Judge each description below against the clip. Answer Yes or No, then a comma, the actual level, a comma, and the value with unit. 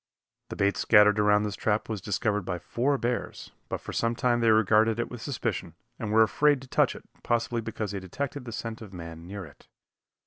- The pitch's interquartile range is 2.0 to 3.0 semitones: Yes, narrow, 2.5 semitones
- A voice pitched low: Yes, low, 110 Hz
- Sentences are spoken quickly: Yes, fast, 210 wpm